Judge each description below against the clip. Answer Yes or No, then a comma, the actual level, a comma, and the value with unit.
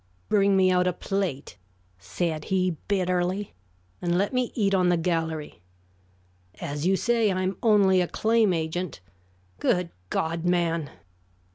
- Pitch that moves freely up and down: No, average, 2.8 semitones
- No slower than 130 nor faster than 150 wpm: Yes, average, 140 wpm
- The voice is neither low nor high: Yes, medium, 180 Hz